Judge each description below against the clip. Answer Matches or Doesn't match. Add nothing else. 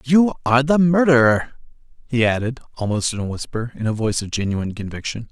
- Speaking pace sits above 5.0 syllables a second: Matches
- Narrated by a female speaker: Doesn't match